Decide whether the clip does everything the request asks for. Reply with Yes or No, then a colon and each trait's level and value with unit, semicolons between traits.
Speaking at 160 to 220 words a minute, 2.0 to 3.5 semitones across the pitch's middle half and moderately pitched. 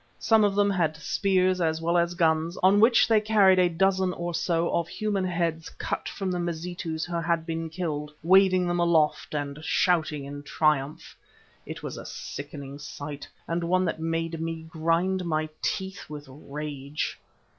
Yes: average, 170 wpm; average, 2.9 semitones; medium, 170 Hz